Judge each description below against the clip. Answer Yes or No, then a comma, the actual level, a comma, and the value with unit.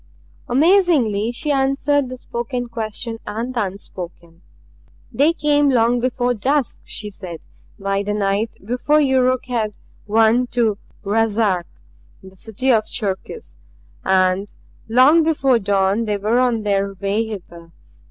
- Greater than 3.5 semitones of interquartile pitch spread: Yes, average, 4.3 semitones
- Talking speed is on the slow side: Yes, slow, 130 wpm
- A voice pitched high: Yes, high, 225 Hz